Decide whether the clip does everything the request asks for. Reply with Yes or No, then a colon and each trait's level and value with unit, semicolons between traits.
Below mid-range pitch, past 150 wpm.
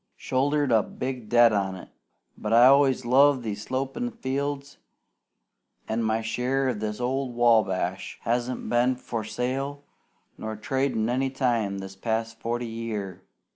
No: low, 120 Hz; average, 140 wpm